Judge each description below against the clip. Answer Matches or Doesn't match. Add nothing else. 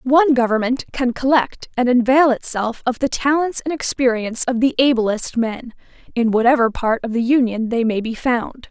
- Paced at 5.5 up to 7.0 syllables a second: Doesn't match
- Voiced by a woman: Matches